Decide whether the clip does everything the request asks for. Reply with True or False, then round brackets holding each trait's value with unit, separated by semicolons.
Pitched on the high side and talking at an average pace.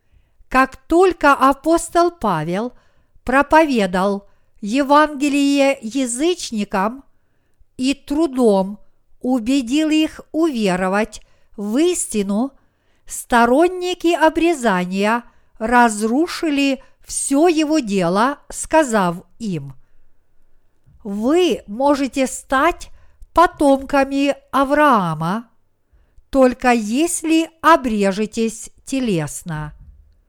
False (260 Hz; 60 wpm)